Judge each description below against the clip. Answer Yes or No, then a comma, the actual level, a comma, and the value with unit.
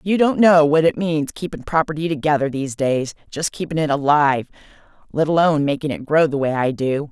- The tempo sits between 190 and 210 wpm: Yes, average, 195 wpm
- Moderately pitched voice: Yes, medium, 150 Hz